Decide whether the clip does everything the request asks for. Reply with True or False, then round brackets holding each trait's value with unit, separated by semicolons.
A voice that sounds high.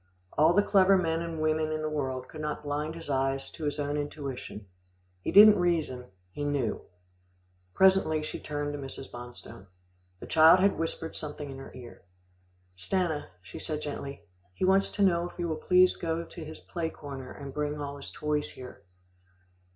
False (150 Hz)